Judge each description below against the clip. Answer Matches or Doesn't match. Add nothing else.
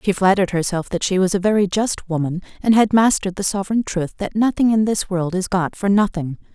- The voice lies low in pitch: Doesn't match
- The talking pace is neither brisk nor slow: Doesn't match